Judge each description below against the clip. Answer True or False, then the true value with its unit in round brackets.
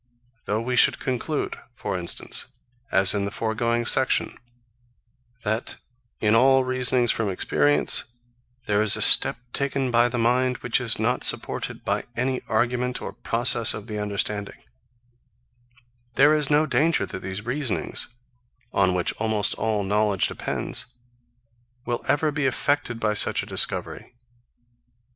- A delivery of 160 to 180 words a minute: False (140 wpm)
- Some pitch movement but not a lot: True (3.6 semitones)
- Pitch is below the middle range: True (115 Hz)